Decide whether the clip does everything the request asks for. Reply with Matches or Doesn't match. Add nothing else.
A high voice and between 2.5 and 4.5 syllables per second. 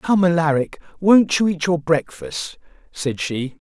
Doesn't match